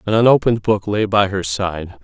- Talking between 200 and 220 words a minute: Yes, fast, 205 wpm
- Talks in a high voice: No, low, 100 Hz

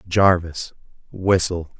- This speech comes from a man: Yes, male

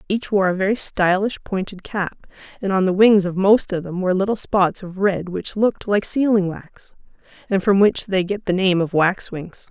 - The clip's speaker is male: No, female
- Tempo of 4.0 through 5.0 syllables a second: Yes, 4.8 syllables/s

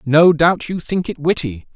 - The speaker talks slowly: No, fast, 205 wpm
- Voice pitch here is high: No, medium, 155 Hz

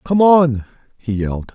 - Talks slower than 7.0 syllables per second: Yes, 4.4 syllables/s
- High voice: No, low, 135 Hz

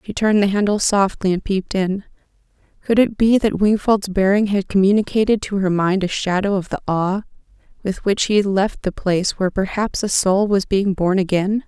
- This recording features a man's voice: No, female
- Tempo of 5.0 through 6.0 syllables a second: Yes, 5.4 syllables/s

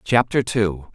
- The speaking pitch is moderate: No, low, 105 Hz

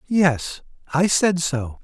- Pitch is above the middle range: No, medium, 165 Hz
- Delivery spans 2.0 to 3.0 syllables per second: Yes, 2.8 syllables/s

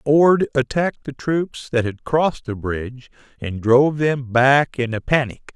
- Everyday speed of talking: Yes, average, 175 wpm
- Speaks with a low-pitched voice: Yes, low, 130 Hz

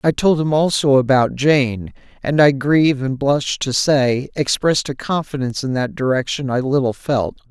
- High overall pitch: No, low, 135 Hz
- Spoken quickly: No, average, 175 wpm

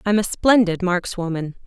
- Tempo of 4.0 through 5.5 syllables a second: Yes, 4.8 syllables/s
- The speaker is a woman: Yes, female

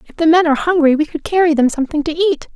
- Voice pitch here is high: Yes, very high, 315 Hz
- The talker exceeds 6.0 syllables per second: Yes, 7.7 syllables/s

